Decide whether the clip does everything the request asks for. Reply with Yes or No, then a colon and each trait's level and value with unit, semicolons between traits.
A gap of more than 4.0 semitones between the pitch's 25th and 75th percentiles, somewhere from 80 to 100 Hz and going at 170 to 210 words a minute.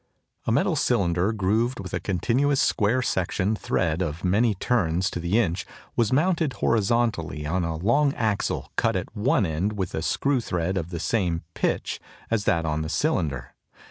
Yes: wide, 5.5 semitones; very low, 95 Hz; average, 175 wpm